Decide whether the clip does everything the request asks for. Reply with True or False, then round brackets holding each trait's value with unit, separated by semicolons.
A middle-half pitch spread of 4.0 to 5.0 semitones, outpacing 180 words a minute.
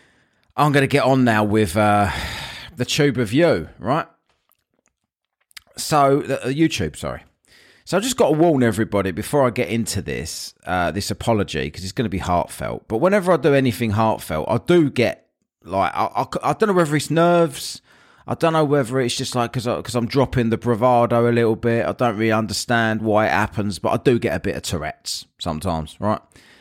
True (4.5 semitones; 200 wpm)